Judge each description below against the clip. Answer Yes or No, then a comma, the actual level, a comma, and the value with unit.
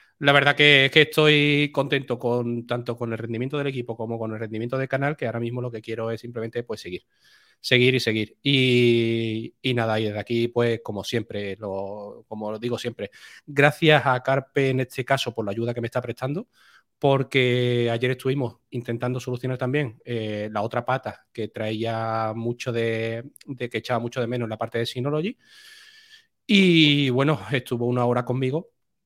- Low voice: Yes, low, 120 Hz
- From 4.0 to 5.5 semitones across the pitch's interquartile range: No, average, 3.0 semitones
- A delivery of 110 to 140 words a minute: No, fast, 190 wpm